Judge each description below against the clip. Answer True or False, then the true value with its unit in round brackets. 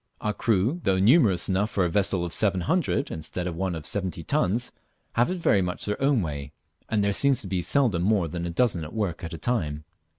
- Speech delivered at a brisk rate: True (225 wpm)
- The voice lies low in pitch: True (95 Hz)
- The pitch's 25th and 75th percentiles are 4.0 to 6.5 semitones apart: True (4.4 semitones)